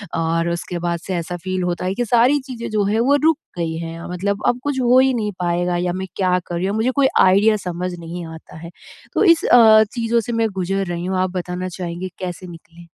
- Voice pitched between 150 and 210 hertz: Yes, medium, 185 Hz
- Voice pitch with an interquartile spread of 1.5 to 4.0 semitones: No, average, 4.7 semitones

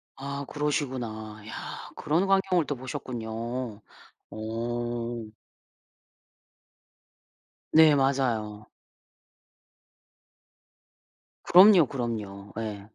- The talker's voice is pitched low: Yes, low, 120 Hz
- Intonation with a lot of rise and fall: No, average, 4.4 semitones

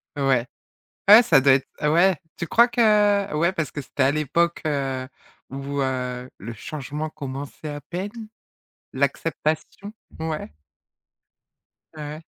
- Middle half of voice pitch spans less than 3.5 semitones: No, average, 4.0 semitones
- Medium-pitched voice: Yes, medium, 150 Hz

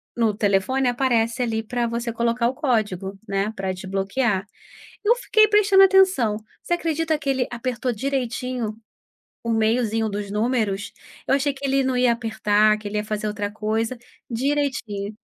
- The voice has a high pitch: Yes, high, 230 Hz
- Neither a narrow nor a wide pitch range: Yes, average, 3.9 semitones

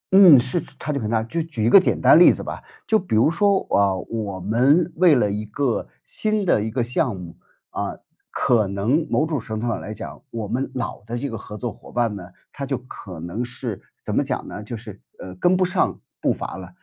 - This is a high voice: No, low, 120 Hz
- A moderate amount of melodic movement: No, wide, 6.0 semitones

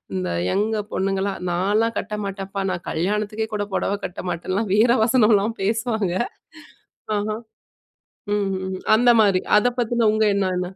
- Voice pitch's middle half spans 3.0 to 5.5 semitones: No, narrow, 2.5 semitones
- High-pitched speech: Yes, high, 205 Hz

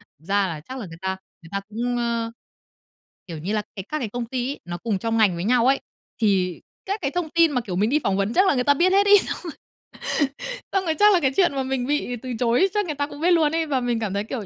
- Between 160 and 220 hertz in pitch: No, high, 245 Hz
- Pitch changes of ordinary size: No, wide, 6.8 semitones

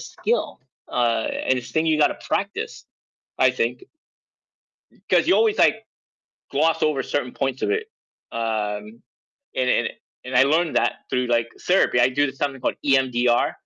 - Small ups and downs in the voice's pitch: No, average, 3.4 semitones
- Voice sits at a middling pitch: No, low, 130 Hz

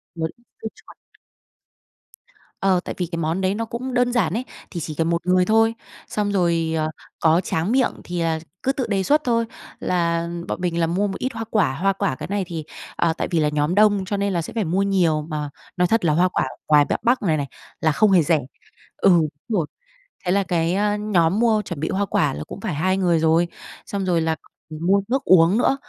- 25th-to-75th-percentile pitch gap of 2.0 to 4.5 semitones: Yes, average, 4.0 semitones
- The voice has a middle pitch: Yes, medium, 180 Hz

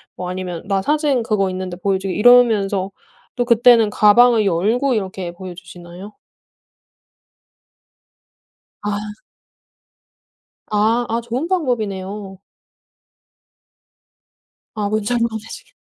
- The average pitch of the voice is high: Yes, high, 210 Hz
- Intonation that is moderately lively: Yes, average, 4.0 semitones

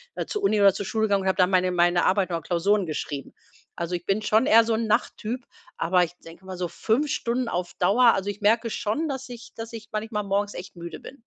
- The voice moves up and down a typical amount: Yes, average, 3.9 semitones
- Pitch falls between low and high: No, high, 205 Hz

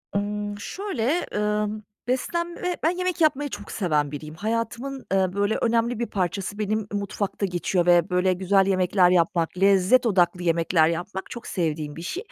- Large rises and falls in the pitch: No, average, 4.6 semitones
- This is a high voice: Yes, high, 200 Hz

